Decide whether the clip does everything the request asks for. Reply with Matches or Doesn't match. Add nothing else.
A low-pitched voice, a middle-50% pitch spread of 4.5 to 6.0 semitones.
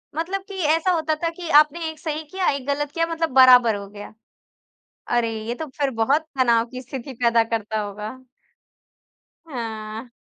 Doesn't match